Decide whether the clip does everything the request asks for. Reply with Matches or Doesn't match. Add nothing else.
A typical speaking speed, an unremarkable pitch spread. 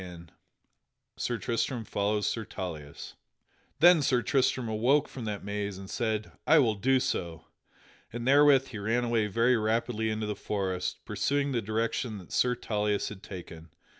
Matches